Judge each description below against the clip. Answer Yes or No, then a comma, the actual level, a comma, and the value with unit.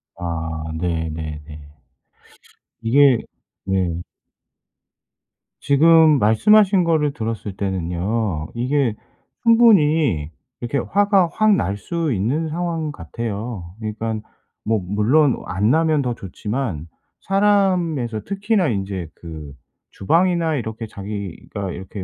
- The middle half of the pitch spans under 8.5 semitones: No, wide, 9.0 semitones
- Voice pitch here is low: Yes, low, 115 Hz